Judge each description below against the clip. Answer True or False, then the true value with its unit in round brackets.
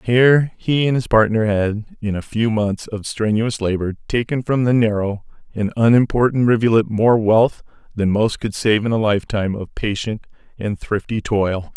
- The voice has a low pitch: True (110 Hz)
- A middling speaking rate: True (175 wpm)